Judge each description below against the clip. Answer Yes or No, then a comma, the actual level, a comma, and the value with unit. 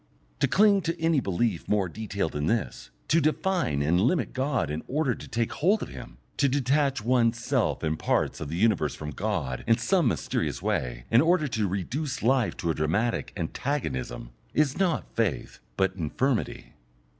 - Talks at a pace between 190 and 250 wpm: No, average, 175 wpm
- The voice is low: Yes, low, 115 Hz